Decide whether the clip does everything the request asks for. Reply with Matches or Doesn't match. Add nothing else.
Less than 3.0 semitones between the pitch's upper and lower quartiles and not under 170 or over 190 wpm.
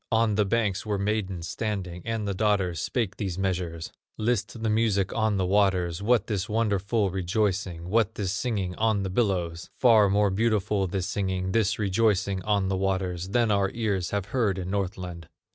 Matches